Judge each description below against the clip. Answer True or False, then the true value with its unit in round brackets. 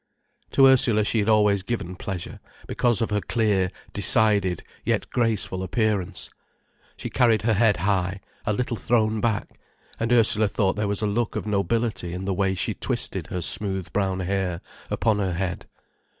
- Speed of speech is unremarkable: True (165 wpm)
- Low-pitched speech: True (105 Hz)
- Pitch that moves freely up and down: False (2.8 semitones)